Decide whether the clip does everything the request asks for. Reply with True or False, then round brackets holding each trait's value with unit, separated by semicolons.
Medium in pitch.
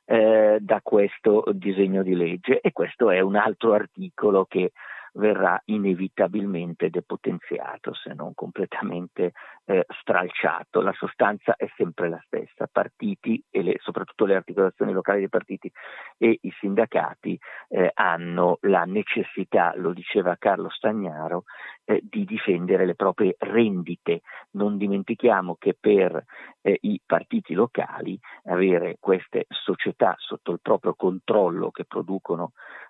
False (100 Hz)